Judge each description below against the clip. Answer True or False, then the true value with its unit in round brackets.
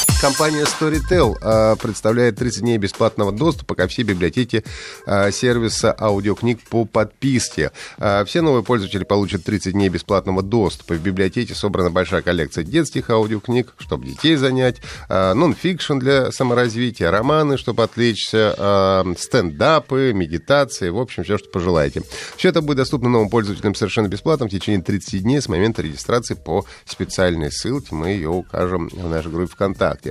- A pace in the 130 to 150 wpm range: True (140 wpm)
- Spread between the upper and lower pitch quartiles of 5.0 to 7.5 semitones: False (4.6 semitones)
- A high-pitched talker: False (110 Hz)